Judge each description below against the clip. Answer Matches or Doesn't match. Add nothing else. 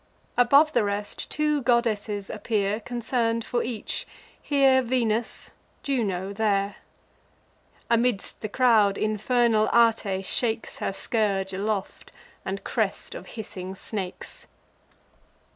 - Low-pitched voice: Doesn't match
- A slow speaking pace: Matches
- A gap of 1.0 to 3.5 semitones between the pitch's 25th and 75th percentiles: Matches